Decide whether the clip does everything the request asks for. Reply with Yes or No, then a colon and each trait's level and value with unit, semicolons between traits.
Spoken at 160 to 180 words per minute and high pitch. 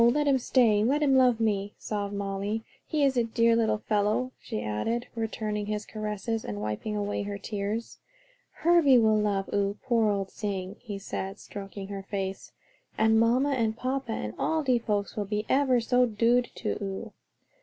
Yes: average, 175 wpm; high, 215 Hz